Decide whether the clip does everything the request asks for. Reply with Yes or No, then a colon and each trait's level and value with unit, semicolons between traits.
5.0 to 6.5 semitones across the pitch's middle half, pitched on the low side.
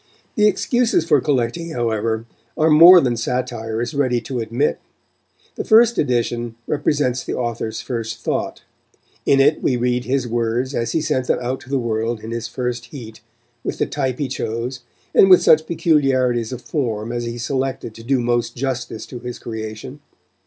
No: average, 3.1 semitones; low, 125 Hz